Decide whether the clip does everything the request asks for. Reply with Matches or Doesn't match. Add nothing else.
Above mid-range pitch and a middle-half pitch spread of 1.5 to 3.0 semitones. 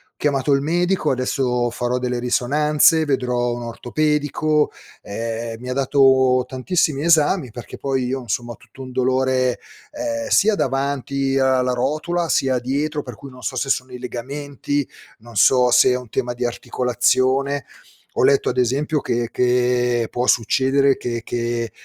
Doesn't match